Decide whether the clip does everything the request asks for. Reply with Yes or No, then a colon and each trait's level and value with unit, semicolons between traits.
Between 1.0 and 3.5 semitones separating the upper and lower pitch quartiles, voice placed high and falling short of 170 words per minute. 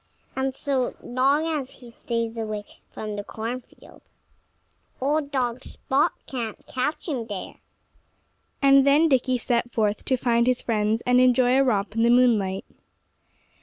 Yes: average, 2.8 semitones; high, 245 Hz; average, 145 wpm